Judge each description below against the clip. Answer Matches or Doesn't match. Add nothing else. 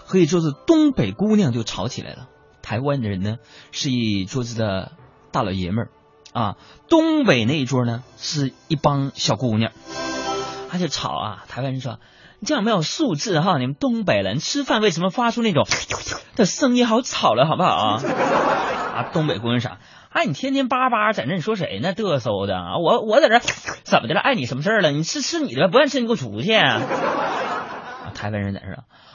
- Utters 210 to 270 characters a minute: Doesn't match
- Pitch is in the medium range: Matches